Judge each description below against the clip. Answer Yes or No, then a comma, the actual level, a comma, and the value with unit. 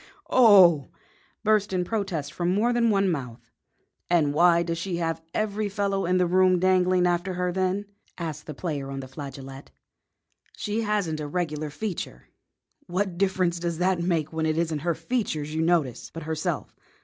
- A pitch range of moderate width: Yes, average, 3.3 semitones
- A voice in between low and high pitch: Yes, medium, 175 Hz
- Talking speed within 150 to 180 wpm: Yes, average, 170 wpm